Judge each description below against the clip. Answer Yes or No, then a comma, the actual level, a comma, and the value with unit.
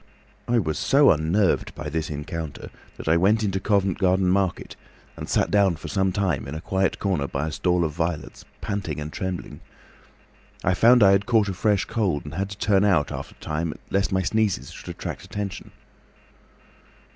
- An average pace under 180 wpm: No, average, 190 wpm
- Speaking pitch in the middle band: No, very low, 95 Hz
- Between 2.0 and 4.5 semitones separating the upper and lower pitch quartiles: Yes, average, 4.0 semitones